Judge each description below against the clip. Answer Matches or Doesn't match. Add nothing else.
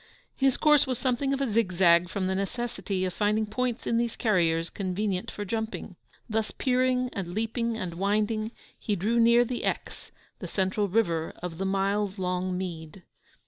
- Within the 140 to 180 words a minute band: Matches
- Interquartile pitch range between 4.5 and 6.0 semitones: Doesn't match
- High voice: Matches